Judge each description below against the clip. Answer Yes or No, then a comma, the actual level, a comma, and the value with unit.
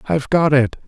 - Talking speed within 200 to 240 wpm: Yes, fast, 205 wpm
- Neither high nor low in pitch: Yes, medium, 145 Hz